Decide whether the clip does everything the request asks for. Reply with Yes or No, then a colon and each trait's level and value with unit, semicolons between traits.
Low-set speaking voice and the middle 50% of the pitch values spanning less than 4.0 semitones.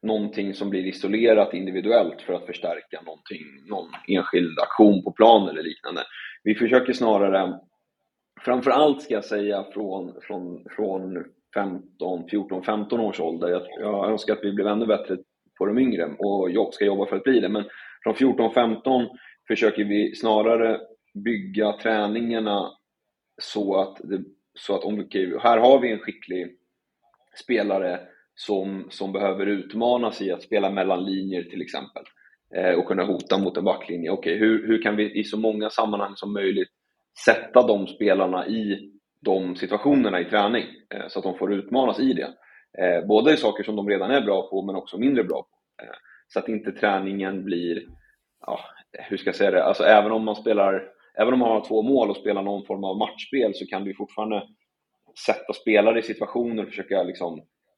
Yes: low, 105 Hz; narrow, 2.4 semitones